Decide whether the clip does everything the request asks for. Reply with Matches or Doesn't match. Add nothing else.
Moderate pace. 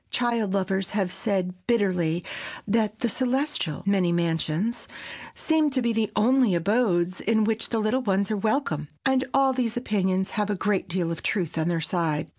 Matches